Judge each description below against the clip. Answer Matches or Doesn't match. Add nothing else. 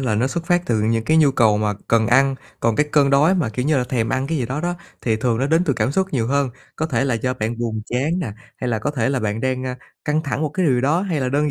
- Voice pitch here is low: Matches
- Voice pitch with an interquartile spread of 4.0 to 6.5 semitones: Matches